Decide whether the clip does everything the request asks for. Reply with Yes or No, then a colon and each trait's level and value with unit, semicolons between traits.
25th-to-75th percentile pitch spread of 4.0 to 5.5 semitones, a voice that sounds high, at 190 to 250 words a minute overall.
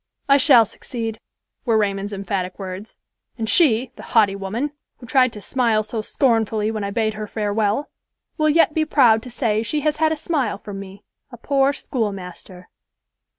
No: average, 4.5 semitones; high, 225 Hz; average, 180 wpm